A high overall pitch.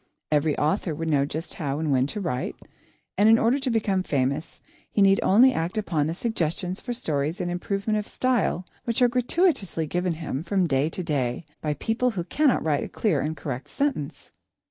No: medium, 175 Hz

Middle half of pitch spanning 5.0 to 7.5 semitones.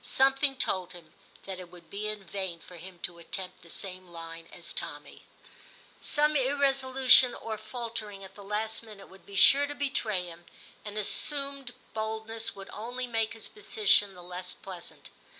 Yes: wide, 5.6 semitones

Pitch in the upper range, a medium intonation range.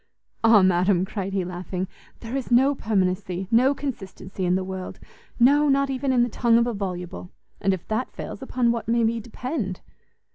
Yes: high, 220 Hz; average, 4.9 semitones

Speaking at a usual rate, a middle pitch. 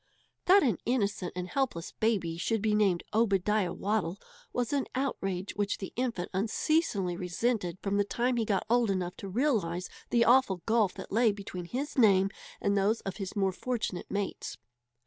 No: average, 170 wpm; high, 205 Hz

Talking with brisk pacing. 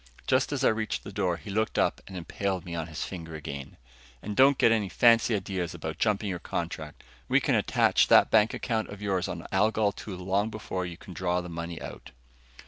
Yes: fast, 215 wpm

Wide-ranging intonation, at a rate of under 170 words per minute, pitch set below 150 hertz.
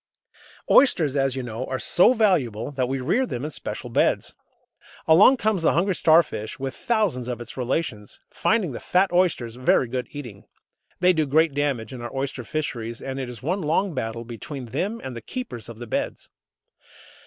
No: wide, 6.0 semitones; average, 185 wpm; low, 135 Hz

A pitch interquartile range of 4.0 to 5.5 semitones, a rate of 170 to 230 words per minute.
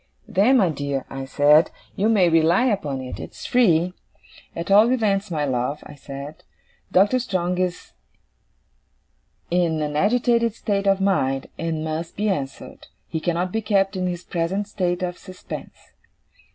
No: average, 4.5 semitones; average, 150 wpm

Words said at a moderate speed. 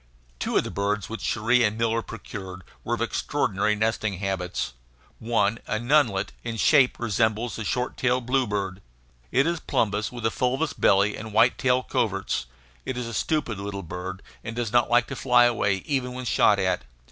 Yes: average, 180 wpm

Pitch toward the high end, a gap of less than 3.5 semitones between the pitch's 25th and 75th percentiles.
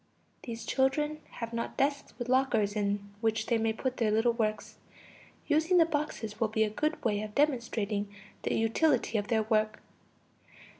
No: high, 230 Hz; average, 3.8 semitones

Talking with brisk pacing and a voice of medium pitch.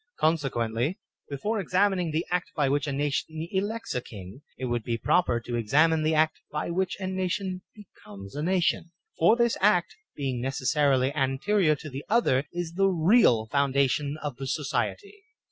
No: average, 170 wpm; medium, 155 Hz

